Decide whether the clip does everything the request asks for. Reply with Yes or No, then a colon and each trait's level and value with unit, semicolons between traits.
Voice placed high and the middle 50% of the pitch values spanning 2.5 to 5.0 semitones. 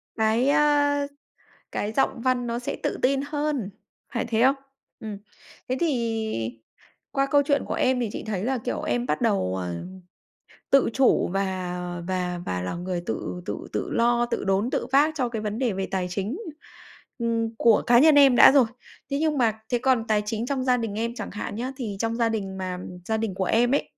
Yes: high, 230 Hz; average, 4.4 semitones